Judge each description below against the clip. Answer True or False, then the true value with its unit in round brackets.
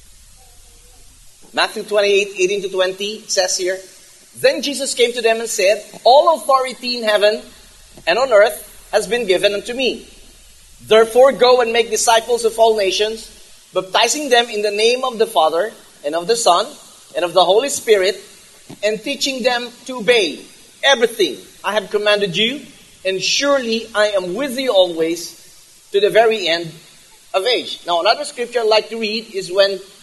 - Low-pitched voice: False (215 Hz)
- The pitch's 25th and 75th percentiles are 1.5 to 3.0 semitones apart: False (4.1 semitones)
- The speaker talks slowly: False (165 wpm)